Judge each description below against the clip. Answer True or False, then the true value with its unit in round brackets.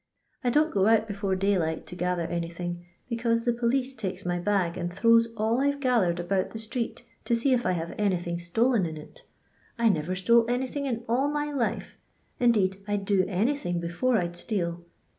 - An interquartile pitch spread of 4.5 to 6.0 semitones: True (5.2 semitones)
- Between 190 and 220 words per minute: True (205 wpm)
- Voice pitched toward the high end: True (205 Hz)